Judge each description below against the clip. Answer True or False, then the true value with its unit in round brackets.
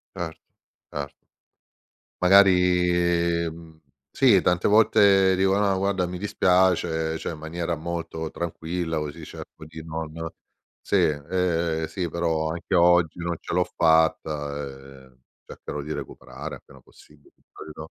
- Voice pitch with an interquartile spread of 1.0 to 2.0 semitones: False (2.4 semitones)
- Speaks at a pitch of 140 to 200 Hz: False (85 Hz)